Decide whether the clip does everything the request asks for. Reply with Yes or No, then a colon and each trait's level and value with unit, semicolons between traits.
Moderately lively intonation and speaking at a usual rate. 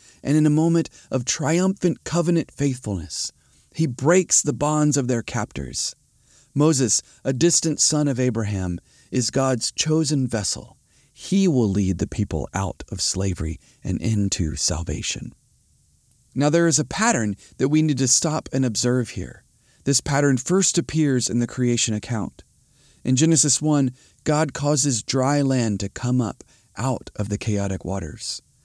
No: wide, 6.2 semitones; average, 150 wpm